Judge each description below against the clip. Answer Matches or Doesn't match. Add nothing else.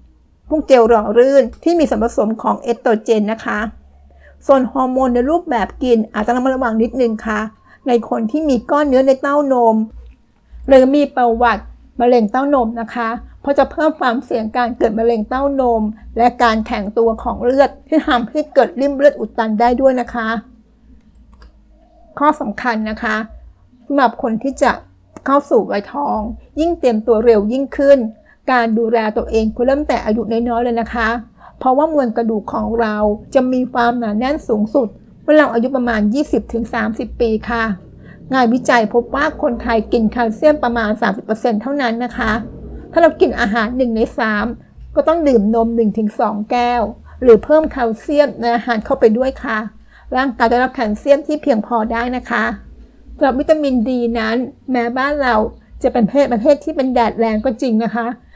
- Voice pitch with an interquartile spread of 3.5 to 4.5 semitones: Doesn't match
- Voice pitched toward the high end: Matches